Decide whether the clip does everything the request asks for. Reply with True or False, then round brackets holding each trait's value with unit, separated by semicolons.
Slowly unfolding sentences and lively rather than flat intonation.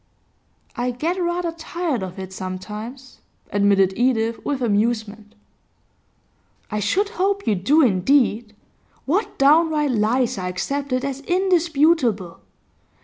True (110 wpm; 7.2 semitones)